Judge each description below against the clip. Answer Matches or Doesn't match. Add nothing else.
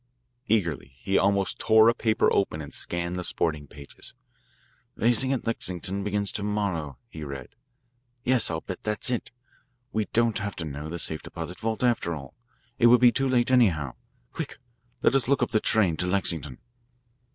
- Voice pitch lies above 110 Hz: Doesn't match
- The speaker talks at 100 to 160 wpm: Doesn't match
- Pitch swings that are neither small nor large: Doesn't match